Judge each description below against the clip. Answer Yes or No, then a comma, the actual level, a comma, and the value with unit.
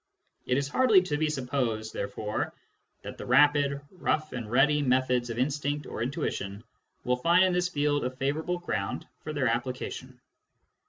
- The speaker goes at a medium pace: Yes, average, 160 wpm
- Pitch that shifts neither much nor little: Yes, average, 3.2 semitones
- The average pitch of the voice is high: No, medium, 140 Hz